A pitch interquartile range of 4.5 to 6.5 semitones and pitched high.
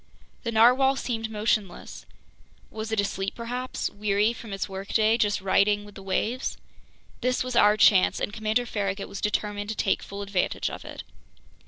No: narrow, 2.4 semitones; high, 210 Hz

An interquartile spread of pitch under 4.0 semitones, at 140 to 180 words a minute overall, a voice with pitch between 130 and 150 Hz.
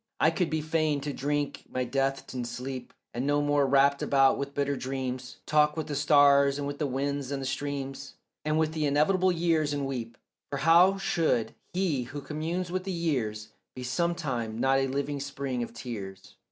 No: narrow, 2.5 semitones; average, 190 wpm; medium, 140 Hz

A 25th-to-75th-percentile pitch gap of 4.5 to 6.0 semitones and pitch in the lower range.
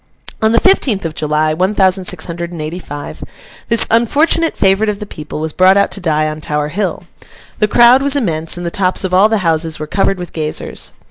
No: average, 5.2 semitones; medium, 185 Hz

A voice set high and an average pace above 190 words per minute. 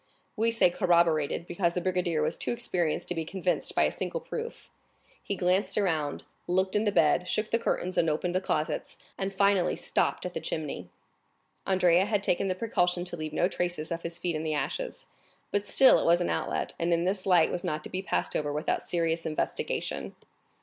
No: medium, 180 Hz; average, 200 wpm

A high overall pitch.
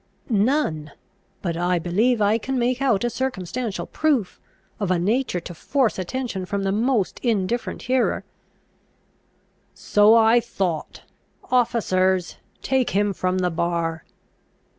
Yes: high, 205 Hz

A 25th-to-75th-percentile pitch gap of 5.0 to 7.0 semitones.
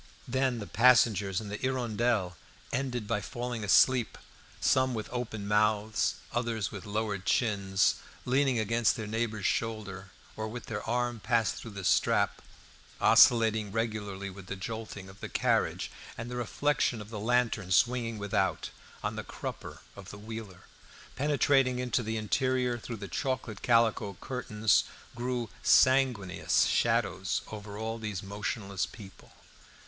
No: average, 3.0 semitones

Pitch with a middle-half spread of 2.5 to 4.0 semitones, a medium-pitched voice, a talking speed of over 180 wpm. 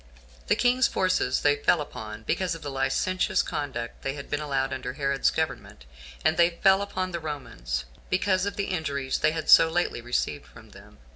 No: wide, 5.6 semitones; medium, 145 Hz; average, 190 wpm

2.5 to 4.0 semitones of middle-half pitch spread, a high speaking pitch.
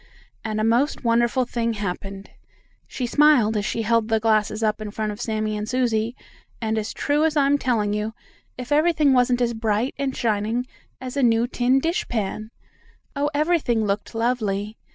Yes: average, 3.0 semitones; high, 230 Hz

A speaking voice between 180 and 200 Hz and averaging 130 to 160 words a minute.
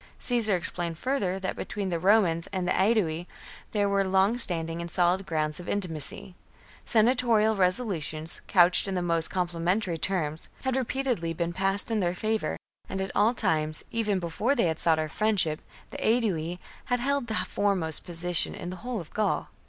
No: medium, 185 Hz; average, 175 wpm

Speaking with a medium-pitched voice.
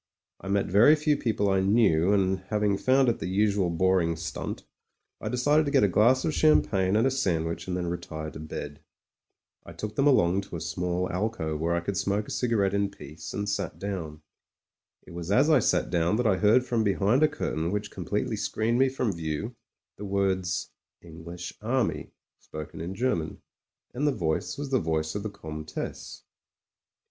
No: low, 100 Hz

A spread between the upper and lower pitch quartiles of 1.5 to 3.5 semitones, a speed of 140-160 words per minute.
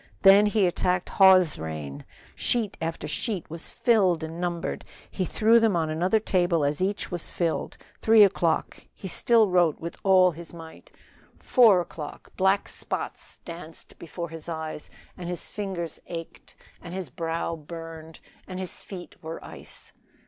Yes: average, 2.8 semitones; average, 155 wpm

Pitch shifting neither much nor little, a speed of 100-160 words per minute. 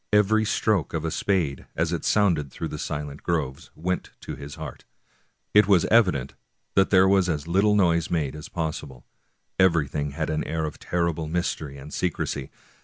No: average, 4.2 semitones; average, 175 wpm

